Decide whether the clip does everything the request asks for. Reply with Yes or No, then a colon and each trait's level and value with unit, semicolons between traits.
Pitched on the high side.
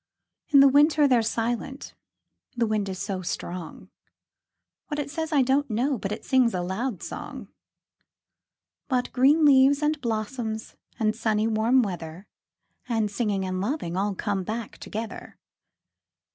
Yes: high, 230 Hz